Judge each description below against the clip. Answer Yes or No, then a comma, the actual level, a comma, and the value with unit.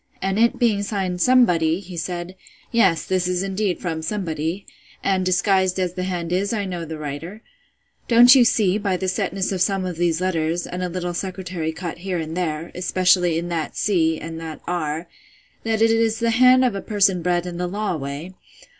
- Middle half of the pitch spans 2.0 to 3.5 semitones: Yes, average, 2.8 semitones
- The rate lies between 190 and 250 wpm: Yes, average, 200 wpm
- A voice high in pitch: No, medium, 180 Hz